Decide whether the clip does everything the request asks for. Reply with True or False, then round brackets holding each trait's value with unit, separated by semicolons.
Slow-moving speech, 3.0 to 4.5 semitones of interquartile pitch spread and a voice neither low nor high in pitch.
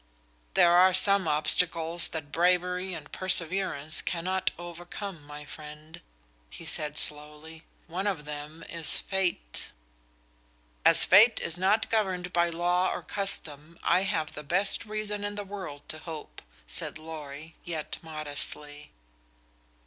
True (130 wpm; 3.6 semitones; 170 Hz)